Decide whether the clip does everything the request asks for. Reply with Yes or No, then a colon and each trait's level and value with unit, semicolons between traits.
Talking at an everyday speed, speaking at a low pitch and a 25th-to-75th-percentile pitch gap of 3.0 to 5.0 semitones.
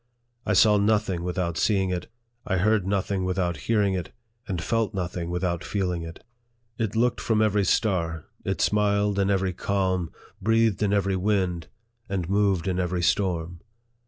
No: average, 160 wpm; very low, 95 Hz; narrow, 2.6 semitones